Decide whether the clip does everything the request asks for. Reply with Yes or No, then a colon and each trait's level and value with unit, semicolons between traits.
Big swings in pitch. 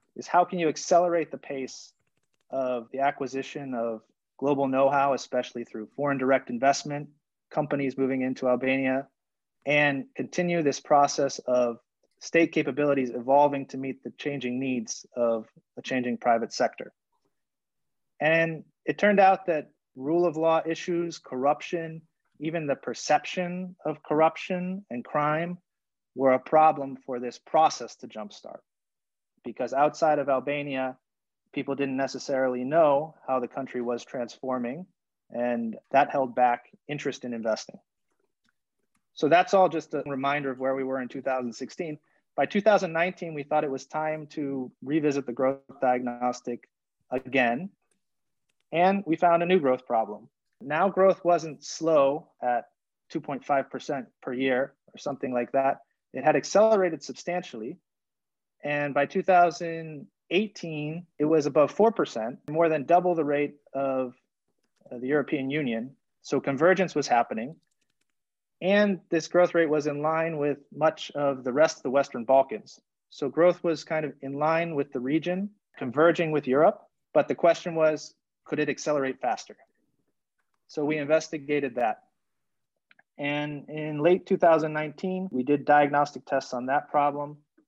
No: average, 3.5 semitones